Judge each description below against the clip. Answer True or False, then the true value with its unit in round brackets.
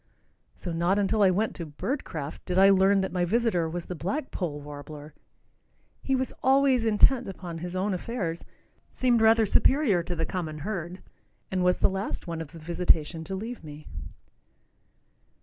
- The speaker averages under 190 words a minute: True (170 wpm)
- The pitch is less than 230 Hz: True (185 Hz)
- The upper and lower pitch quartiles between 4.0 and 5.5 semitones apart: True (4.8 semitones)